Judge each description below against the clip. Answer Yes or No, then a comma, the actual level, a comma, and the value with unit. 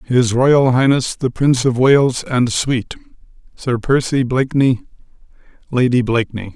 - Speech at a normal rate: No, slow, 130 wpm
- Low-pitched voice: Yes, low, 125 Hz